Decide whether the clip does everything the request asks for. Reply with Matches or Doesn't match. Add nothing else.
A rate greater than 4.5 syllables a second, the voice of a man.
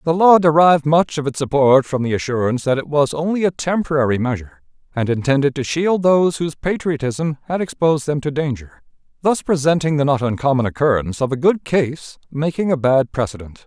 Matches